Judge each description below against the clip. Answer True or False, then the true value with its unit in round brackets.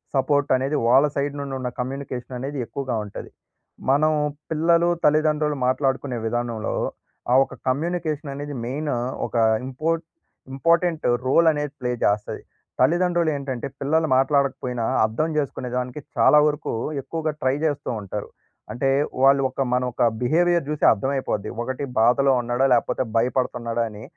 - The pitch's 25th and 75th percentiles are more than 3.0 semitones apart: True (3.4 semitones)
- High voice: False (135 Hz)